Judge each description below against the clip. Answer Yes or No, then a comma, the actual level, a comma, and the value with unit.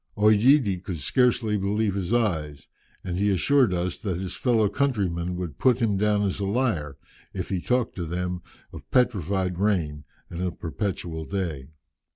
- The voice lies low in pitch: Yes, very low, 95 Hz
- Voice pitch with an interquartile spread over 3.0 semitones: Yes, average, 3.7 semitones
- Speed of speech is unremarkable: Yes, average, 165 wpm